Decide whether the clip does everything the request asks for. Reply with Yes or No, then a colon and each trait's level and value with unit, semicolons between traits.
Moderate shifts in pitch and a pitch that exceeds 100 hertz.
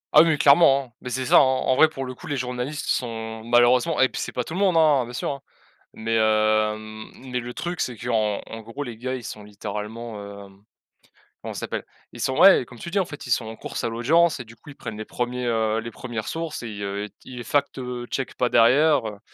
Yes: average, 3.8 semitones; low, 120 Hz